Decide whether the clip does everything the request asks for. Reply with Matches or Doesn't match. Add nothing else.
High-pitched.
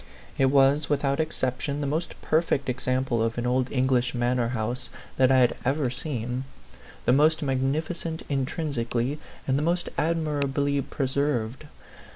Doesn't match